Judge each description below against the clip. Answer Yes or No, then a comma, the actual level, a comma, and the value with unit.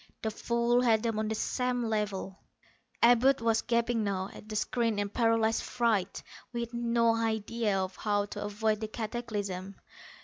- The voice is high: Yes, high, 225 Hz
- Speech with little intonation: Yes, narrow, 2.2 semitones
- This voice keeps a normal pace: Yes, average, 160 wpm